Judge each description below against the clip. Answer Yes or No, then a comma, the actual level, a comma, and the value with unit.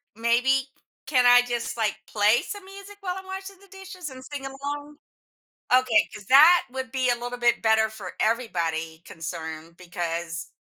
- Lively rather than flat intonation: Yes, wide, 6.0 semitones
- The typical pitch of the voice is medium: No, high, 245 Hz